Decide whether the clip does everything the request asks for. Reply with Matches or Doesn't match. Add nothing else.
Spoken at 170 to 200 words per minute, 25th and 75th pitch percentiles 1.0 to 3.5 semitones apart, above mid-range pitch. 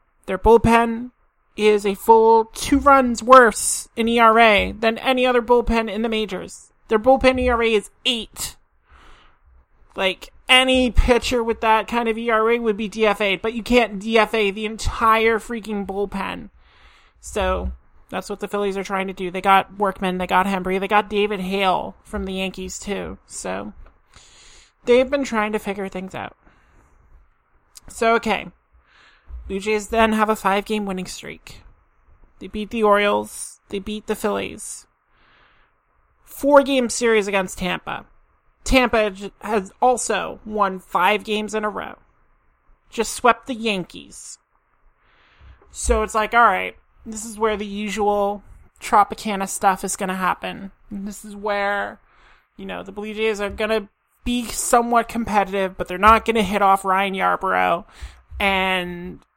Doesn't match